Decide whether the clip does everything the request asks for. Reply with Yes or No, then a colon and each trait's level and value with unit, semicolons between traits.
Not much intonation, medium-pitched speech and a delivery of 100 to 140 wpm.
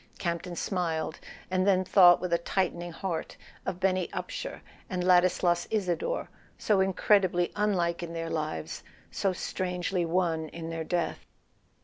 Yes: narrow, 1.7 semitones; medium, 180 Hz; slow, 135 wpm